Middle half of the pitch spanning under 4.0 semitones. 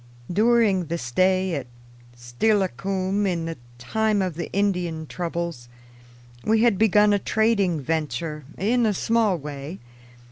No: average, 4.4 semitones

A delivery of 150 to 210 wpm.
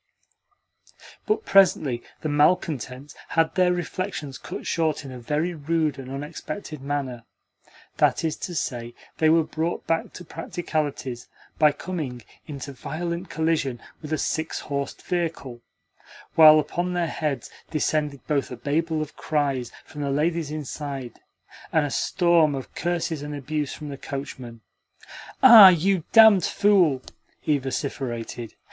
No: average, 140 wpm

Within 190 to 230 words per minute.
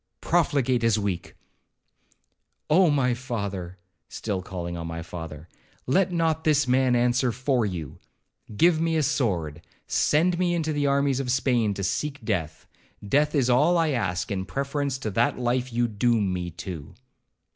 No: average, 150 wpm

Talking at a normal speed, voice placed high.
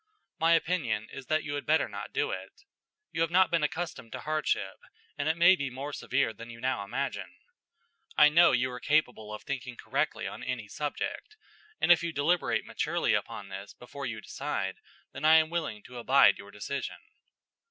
No: average, 190 wpm; medium, 140 Hz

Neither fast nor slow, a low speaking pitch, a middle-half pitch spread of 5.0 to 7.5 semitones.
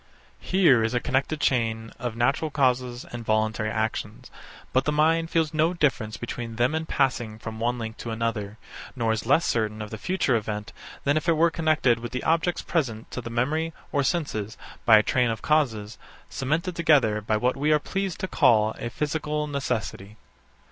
Yes: average, 190 wpm; low, 125 Hz; wide, 5.5 semitones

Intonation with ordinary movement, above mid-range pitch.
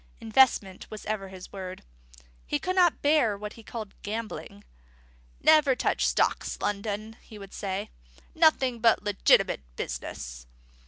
Yes: average, 3.8 semitones; high, 215 Hz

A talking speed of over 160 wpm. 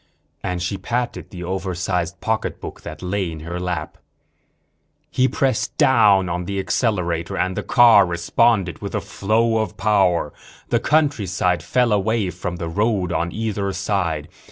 No: average, 150 wpm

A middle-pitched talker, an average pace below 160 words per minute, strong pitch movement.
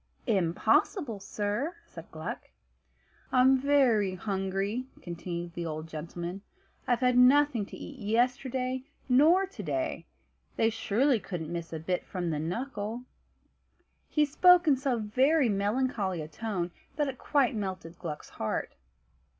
No: high, 215 Hz; slow, 135 wpm; wide, 6.7 semitones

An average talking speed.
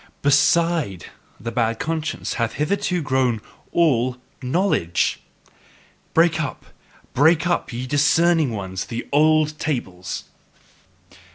No: slow, 100 wpm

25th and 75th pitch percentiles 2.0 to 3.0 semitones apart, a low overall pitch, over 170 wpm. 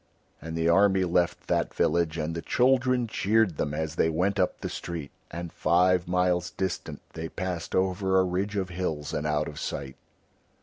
Yes: narrow, 2.6 semitones; very low, 90 Hz; average, 180 wpm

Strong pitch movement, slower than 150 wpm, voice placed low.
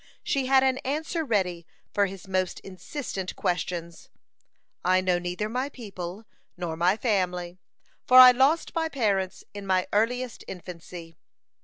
No: wide, 5.9 semitones; average, 140 wpm; high, 195 Hz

